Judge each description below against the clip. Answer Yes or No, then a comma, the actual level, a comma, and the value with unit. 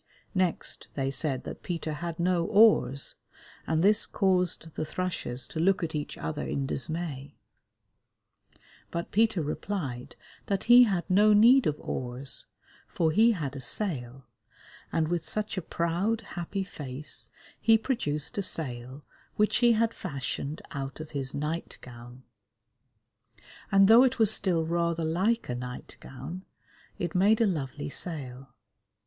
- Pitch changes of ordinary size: No, wide, 5.9 semitones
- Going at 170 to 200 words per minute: No, average, 145 wpm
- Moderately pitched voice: Yes, medium, 165 Hz